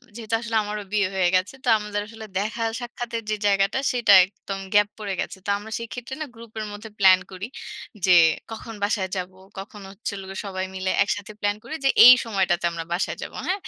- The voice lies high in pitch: Yes, high, 205 Hz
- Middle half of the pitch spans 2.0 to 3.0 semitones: Yes, average, 2.7 semitones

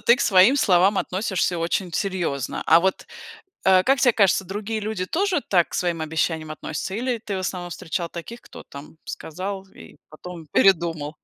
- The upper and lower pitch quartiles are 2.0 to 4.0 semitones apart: Yes, average, 3.6 semitones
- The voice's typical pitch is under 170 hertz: No, medium, 185 Hz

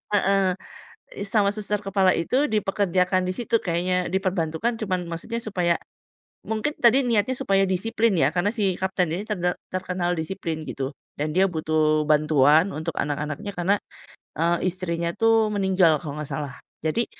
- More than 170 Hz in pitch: Yes, medium, 185 Hz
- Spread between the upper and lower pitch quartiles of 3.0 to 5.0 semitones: Yes, average, 3.8 semitones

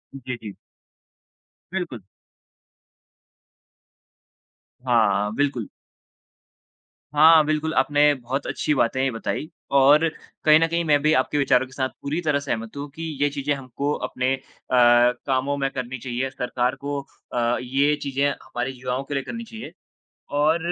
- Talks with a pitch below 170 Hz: Yes, low, 135 Hz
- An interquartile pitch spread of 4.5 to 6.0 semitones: No, average, 2.8 semitones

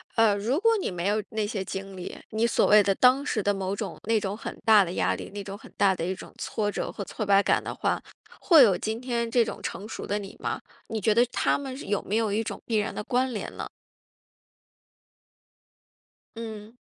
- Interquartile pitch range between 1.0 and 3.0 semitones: Yes, narrow, 2.5 semitones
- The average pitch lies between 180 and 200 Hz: No, high, 210 Hz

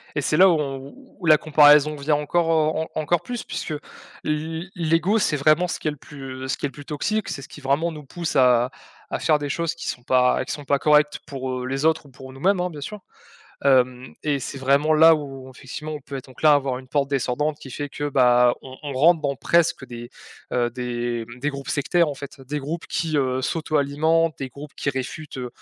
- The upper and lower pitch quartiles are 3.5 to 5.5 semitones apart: No, average, 2.9 semitones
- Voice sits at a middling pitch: Yes, medium, 145 Hz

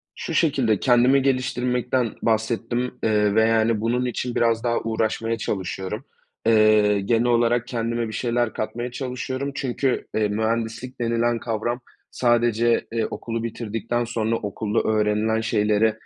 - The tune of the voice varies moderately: No, narrow, 1.7 semitones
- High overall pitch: No, low, 115 Hz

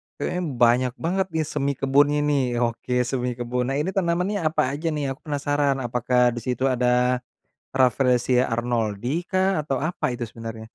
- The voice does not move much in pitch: No, average, 3.3 semitones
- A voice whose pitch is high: No, low, 130 Hz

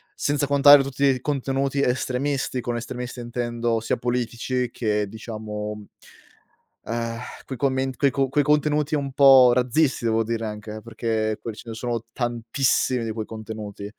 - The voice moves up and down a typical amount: Yes, average, 3.1 semitones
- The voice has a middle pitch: No, low, 120 Hz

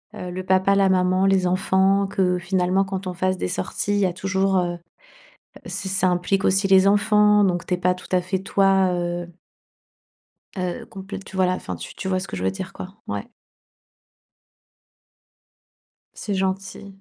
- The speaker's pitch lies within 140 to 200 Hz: Yes, high, 190 Hz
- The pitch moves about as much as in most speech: No, narrow, 1.2 semitones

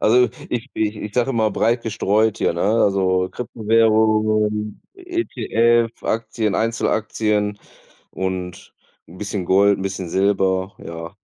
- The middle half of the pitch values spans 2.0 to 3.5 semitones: Yes, average, 2.7 semitones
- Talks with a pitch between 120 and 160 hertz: No, low, 105 Hz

